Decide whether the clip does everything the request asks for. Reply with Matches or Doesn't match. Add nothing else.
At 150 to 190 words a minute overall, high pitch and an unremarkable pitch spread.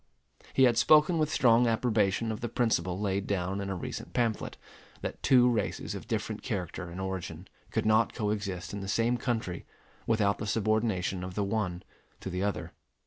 Doesn't match